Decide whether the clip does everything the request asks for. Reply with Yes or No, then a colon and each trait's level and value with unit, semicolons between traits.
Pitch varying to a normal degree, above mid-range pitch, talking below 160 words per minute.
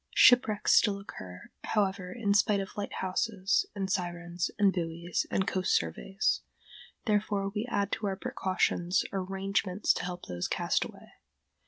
No: narrow, 2.2 semitones; high, 195 Hz; average, 145 wpm